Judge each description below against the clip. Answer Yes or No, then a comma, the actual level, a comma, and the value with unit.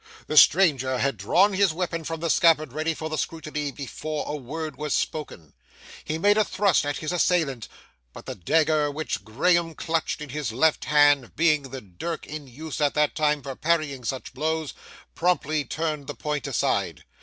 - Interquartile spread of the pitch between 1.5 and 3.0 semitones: Yes, average, 2.7 semitones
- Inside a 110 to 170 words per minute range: No, average, 180 wpm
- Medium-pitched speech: Yes, medium, 155 Hz